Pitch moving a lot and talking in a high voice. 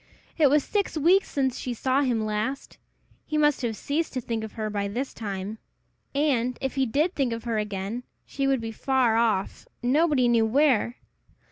No: average, 4.0 semitones; very high, 250 Hz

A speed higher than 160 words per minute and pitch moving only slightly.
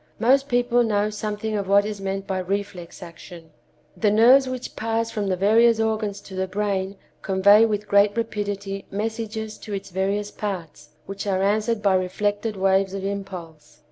Yes: average, 170 wpm; narrow, 2.2 semitones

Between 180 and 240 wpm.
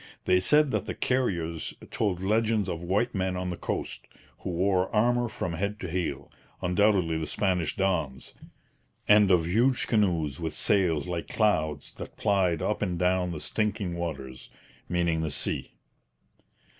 No: average, 155 wpm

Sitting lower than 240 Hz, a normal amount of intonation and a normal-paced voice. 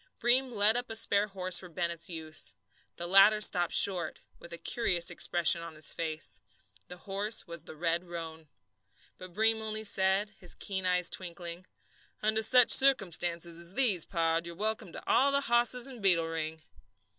Yes: medium, 185 Hz; average, 4.3 semitones; average, 170 wpm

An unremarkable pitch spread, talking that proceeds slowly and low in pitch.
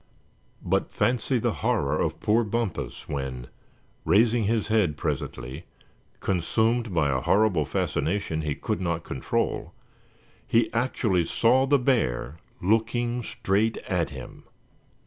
No: wide, 6.8 semitones; slow, 120 wpm; low, 105 Hz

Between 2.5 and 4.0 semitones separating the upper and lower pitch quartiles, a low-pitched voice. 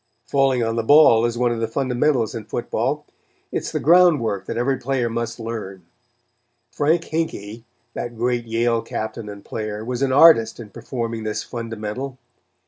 Yes: average, 2.8 semitones; low, 115 Hz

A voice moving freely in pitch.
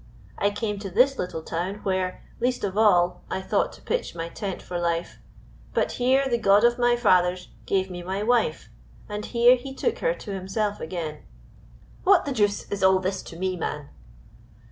No: average, 4.7 semitones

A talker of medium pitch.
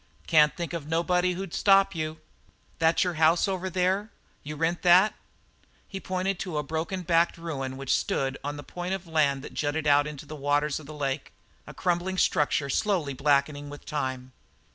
Yes: medium, 160 Hz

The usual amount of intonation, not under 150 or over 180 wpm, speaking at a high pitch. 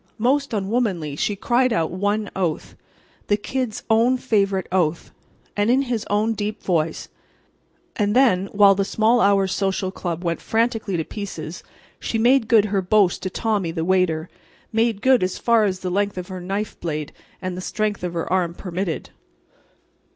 Yes: average, 3.5 semitones; average, 160 wpm; high, 200 Hz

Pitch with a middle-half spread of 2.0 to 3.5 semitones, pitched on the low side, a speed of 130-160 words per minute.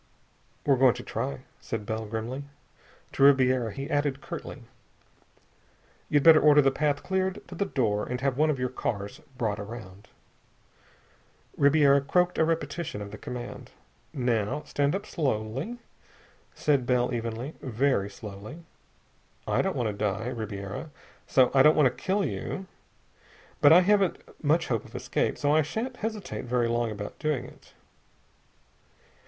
No: wide, 5.4 semitones; low, 130 Hz; average, 150 wpm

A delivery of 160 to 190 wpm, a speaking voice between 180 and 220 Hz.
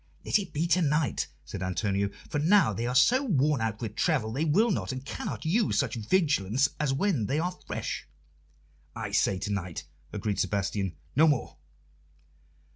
No: average, 175 wpm; low, 135 Hz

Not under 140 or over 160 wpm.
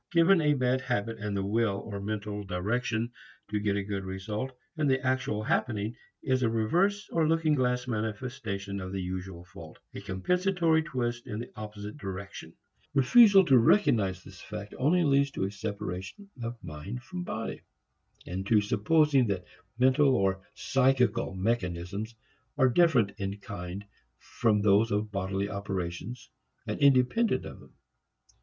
Yes: average, 150 wpm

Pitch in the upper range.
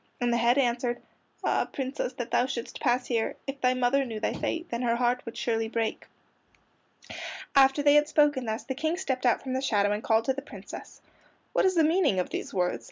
Yes: very high, 250 Hz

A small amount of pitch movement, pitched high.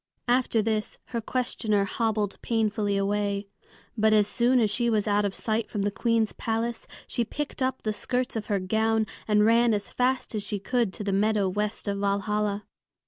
Yes: narrow, 2.2 semitones; high, 215 Hz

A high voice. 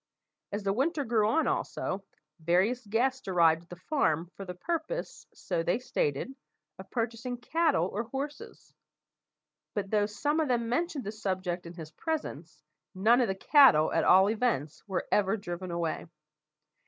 Yes: high, 210 Hz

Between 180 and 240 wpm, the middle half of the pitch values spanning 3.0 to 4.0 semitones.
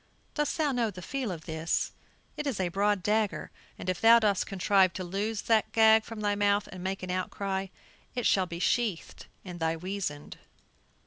Yes: average, 190 wpm; average, 3.3 semitones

